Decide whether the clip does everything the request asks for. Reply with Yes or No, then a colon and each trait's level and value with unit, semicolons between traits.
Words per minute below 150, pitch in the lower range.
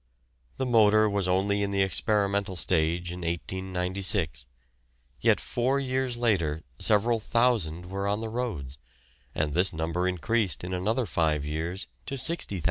Yes: average, 140 wpm; very low, 95 Hz